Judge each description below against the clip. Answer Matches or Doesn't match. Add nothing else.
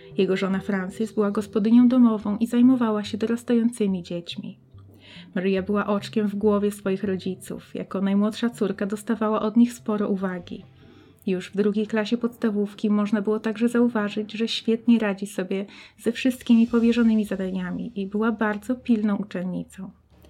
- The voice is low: Doesn't match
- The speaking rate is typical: Matches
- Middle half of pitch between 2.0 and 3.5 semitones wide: Matches